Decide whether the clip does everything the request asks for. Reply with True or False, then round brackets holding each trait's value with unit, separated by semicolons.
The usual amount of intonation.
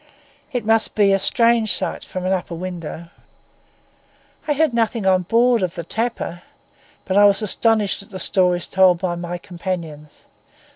True (4.1 semitones)